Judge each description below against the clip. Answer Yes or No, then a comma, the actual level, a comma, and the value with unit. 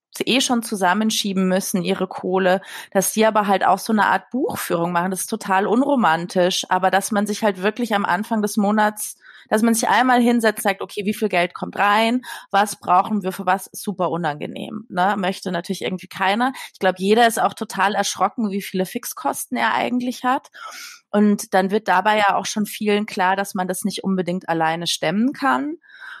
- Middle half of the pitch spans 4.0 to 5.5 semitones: No, average, 2.9 semitones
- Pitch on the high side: Yes, high, 205 Hz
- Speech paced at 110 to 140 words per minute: No, fast, 190 wpm